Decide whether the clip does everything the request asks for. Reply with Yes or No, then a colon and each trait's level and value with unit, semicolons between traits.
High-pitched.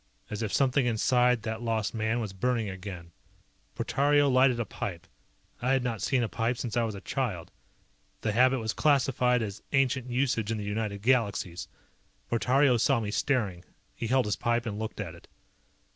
No: low, 115 Hz